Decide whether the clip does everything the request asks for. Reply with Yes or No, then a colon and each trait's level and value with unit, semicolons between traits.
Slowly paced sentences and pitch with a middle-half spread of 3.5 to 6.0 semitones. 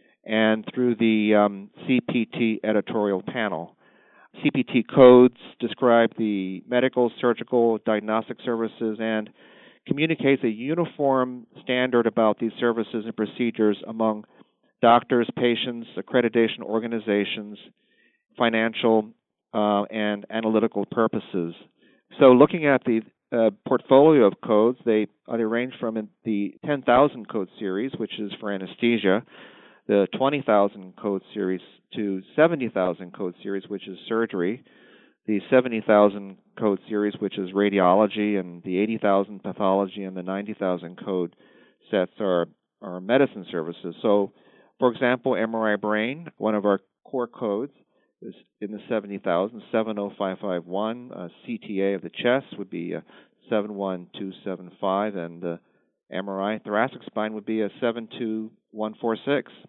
No: slow, 120 wpm; average, 2.8 semitones